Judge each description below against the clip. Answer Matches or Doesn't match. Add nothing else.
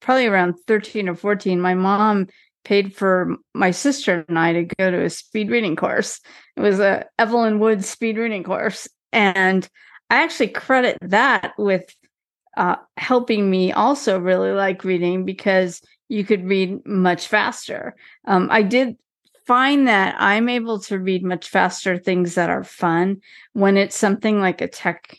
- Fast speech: Doesn't match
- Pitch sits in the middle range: Doesn't match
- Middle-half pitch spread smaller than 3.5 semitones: Matches